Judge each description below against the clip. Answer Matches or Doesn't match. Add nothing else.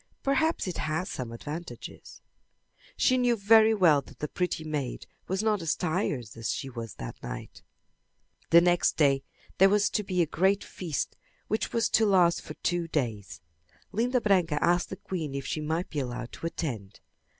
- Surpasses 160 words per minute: Matches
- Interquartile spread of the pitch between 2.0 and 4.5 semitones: Doesn't match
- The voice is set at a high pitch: Doesn't match